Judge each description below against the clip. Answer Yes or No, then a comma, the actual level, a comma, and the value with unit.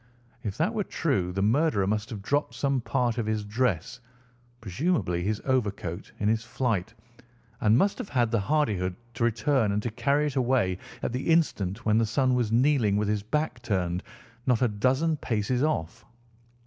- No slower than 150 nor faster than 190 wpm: Yes, average, 180 wpm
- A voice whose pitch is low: Yes, low, 115 Hz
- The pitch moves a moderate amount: Yes, average, 4.5 semitones